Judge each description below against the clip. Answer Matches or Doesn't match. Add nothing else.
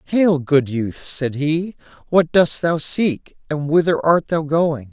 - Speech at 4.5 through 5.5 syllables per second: Doesn't match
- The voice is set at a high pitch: Doesn't match